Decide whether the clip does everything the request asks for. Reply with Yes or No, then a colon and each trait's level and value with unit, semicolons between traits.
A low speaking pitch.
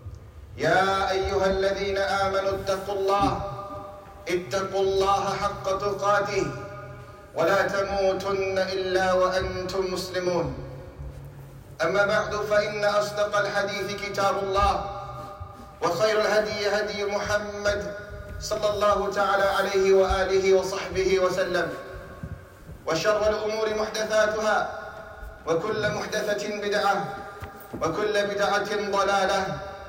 No: high, 195 Hz